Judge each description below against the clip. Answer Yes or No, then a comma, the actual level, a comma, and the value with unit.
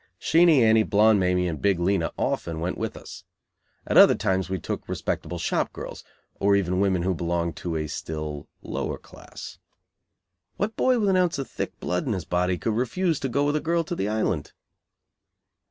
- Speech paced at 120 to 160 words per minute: No, average, 190 wpm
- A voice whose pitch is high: No, very low, 95 Hz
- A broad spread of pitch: Yes, wide, 8.0 semitones